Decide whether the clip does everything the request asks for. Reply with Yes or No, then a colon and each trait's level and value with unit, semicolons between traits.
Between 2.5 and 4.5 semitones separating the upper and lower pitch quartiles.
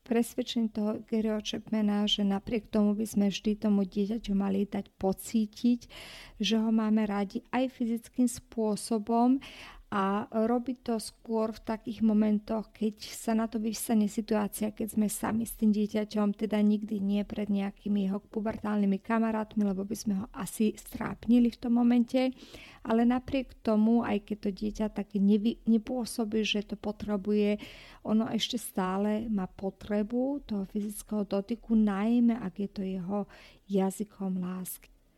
No: narrow, 1.9 semitones